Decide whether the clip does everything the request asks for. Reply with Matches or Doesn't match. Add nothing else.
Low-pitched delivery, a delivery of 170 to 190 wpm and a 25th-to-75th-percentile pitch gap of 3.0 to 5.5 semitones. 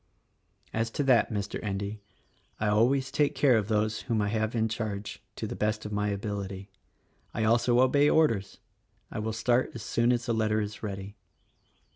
Doesn't match